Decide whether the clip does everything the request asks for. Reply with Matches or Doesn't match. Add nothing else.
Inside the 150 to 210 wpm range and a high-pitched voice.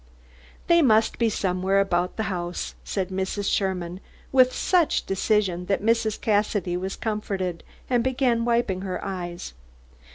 Doesn't match